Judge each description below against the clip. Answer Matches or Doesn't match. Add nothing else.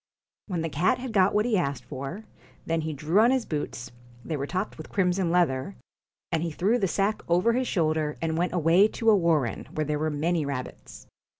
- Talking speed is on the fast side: Matches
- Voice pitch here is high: Doesn't match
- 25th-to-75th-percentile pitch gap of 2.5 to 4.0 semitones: Doesn't match